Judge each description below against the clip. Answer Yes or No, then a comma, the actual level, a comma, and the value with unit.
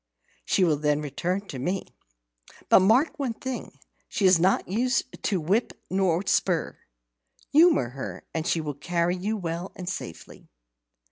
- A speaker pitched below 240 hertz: Yes, medium, 185 Hz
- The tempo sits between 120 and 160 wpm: Yes, average, 150 wpm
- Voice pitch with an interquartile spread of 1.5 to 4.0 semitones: No, average, 4.7 semitones